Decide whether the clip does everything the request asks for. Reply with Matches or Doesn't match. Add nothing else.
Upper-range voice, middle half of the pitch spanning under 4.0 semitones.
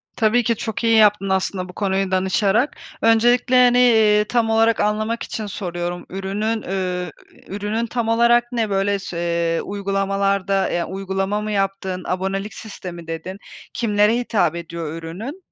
Matches